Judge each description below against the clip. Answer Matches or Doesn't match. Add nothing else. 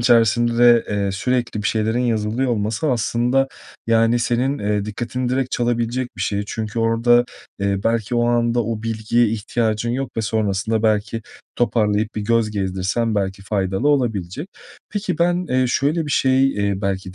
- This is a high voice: Doesn't match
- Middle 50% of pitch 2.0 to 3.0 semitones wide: Matches